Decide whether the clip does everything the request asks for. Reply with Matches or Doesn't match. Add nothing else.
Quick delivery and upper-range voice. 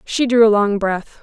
Matches